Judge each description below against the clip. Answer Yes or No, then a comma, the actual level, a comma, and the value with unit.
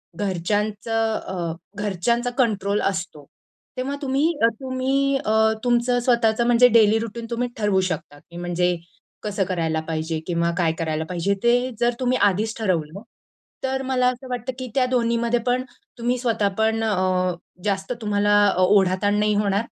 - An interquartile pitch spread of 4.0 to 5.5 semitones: Yes, average, 4.6 semitones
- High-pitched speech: Yes, high, 215 Hz